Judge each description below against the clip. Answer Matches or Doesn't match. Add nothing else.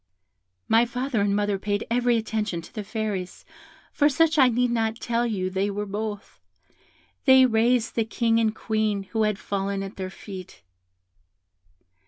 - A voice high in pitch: Matches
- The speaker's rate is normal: Matches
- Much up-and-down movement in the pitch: Doesn't match